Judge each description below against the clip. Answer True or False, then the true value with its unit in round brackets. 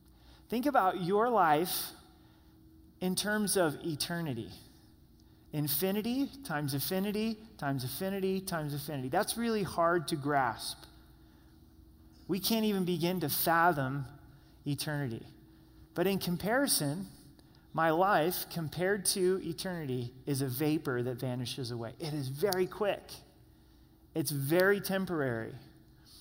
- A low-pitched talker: False (160 Hz)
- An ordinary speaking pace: False (110 wpm)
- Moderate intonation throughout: False (6.6 semitones)